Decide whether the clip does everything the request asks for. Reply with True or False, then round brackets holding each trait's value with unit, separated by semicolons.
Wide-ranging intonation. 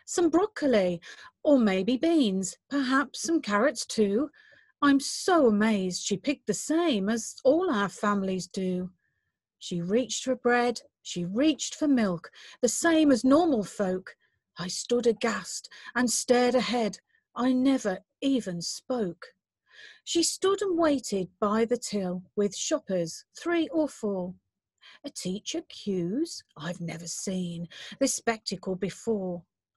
True (7.1 semitones)